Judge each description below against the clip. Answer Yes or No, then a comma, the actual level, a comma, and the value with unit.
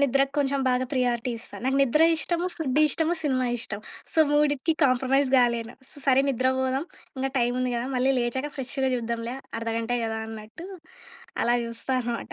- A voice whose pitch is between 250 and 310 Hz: Yes, very high, 255 Hz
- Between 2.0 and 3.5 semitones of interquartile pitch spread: Yes, narrow, 2.5 semitones